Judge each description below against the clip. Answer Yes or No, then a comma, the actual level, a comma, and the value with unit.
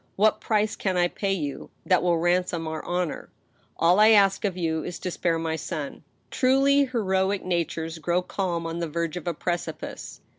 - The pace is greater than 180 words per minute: Yes, average, 190 wpm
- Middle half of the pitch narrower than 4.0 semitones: Yes, average, 2.8 semitones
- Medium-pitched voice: Yes, medium, 175 Hz